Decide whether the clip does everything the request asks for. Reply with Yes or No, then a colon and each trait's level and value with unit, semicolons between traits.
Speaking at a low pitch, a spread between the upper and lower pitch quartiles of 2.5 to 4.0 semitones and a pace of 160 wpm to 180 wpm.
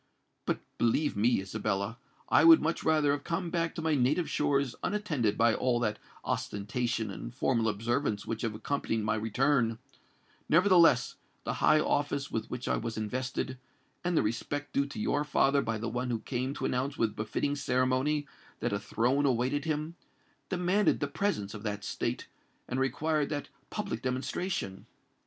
No: low, 130 Hz; average, 4.6 semitones; average, 165 wpm